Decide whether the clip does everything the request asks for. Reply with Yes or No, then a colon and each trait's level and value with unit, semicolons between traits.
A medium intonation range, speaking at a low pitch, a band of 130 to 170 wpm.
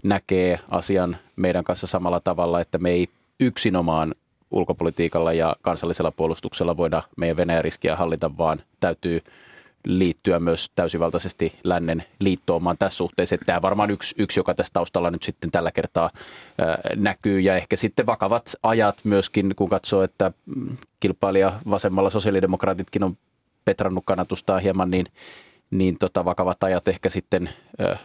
No: narrow, 2.1 semitones; very low, 95 Hz; average, 145 wpm